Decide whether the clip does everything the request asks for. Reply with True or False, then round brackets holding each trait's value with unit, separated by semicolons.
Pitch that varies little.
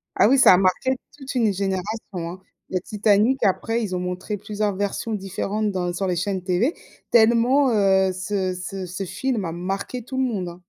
False (3.5 semitones)